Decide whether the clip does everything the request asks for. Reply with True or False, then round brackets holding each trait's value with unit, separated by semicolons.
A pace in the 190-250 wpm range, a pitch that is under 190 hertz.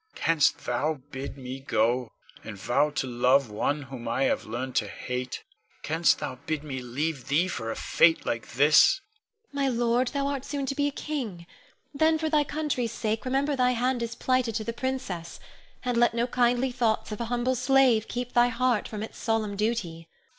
False (195 wpm; 220 Hz)